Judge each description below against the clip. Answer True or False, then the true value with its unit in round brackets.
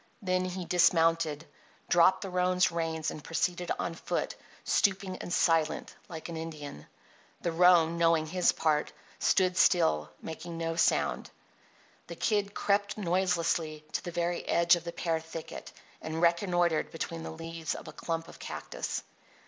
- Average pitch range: False (1.8 semitones)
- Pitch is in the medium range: True (170 Hz)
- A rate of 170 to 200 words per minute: False (150 wpm)